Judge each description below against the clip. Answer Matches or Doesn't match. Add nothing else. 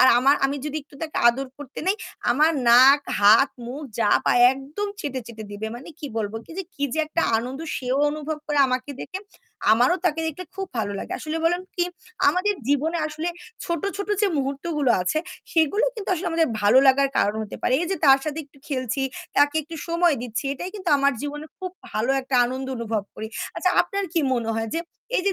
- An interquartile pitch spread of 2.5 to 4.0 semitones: Doesn't match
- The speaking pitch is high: Matches